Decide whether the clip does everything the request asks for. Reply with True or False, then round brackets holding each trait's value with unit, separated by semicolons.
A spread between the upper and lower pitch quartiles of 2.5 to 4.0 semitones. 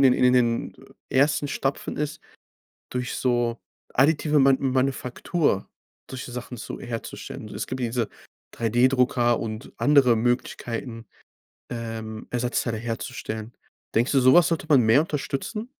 True (2.8 semitones)